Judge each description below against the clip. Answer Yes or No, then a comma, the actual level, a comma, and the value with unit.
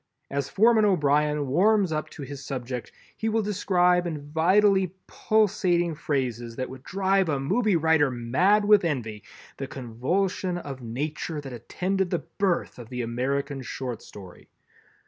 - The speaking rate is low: No, average, 145 wpm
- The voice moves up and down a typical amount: No, wide, 6.5 semitones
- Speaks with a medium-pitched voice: Yes, medium, 155 Hz